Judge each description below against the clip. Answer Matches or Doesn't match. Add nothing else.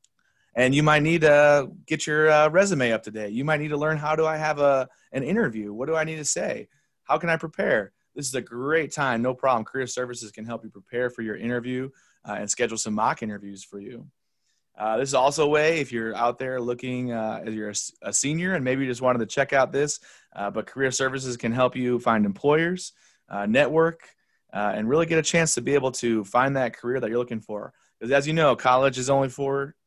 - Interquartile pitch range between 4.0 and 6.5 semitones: Matches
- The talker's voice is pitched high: Doesn't match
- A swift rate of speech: Matches